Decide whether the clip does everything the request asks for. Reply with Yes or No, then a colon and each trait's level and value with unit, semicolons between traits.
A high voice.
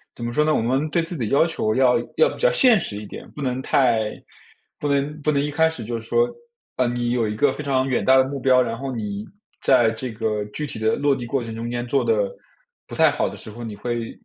No: low, 125 Hz